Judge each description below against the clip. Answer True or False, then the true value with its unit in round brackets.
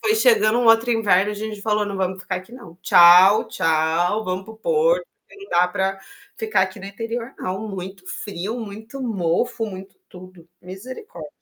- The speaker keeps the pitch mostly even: False (3.5 semitones)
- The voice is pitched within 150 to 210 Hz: True (200 Hz)